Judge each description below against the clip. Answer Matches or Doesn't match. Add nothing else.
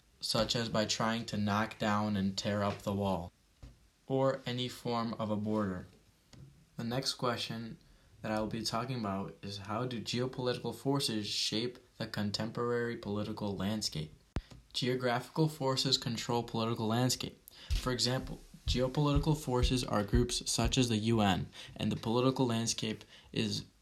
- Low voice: Matches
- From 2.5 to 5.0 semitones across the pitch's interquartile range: Matches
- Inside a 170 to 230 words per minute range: Doesn't match